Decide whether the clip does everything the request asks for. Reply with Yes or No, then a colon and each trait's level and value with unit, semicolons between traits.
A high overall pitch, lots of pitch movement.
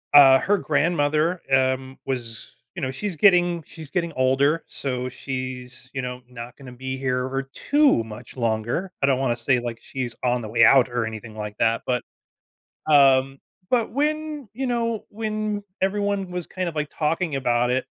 No: low, 135 Hz; wide, 6.2 semitones